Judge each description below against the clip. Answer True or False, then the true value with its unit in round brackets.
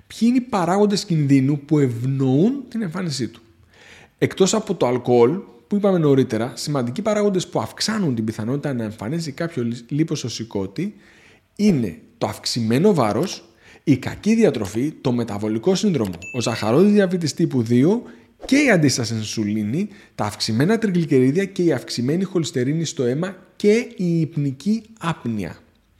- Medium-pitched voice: True (150 Hz)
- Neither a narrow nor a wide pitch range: False (8.3 semitones)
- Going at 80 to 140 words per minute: True (135 wpm)